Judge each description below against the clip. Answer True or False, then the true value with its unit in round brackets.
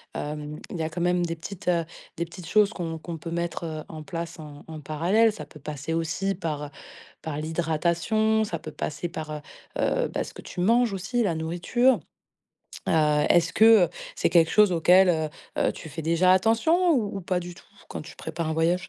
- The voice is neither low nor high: True (170 Hz)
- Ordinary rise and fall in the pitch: True (3.3 semitones)